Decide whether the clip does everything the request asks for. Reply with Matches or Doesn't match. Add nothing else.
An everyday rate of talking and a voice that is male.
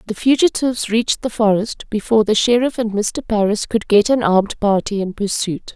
Doesn't match